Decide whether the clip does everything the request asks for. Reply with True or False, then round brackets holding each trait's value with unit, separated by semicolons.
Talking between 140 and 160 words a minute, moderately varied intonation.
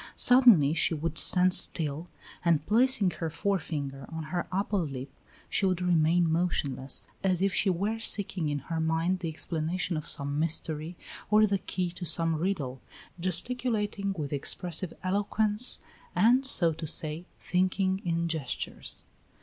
True (145 wpm; 3.6 semitones)